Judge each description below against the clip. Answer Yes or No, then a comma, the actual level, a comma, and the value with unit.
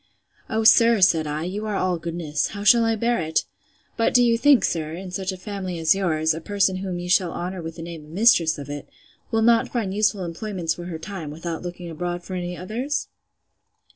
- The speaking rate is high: Yes, fast, 215 wpm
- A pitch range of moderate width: Yes, average, 4.0 semitones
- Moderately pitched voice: Yes, medium, 180 Hz